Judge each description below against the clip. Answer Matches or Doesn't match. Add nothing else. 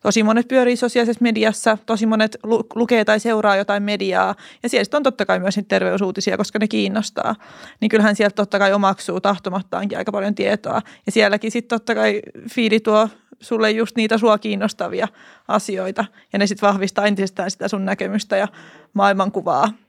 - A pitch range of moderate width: Doesn't match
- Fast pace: Matches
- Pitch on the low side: Doesn't match